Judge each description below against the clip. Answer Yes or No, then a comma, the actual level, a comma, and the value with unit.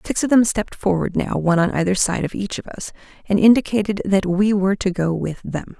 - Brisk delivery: Yes, fast, 240 wpm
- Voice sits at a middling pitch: No, high, 195 Hz